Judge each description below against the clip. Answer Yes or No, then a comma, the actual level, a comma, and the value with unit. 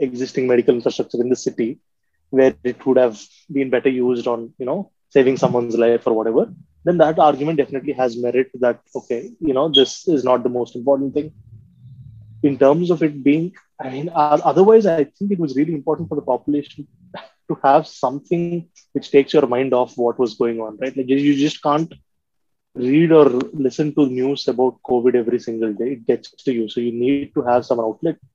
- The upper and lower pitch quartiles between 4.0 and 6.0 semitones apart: No, average, 3.2 semitones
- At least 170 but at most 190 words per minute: No, average, 200 wpm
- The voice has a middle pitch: No, low, 130 Hz